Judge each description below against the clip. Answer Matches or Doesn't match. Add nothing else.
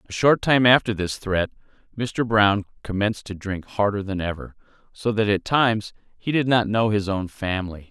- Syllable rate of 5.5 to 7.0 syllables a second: Doesn't match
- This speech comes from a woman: Doesn't match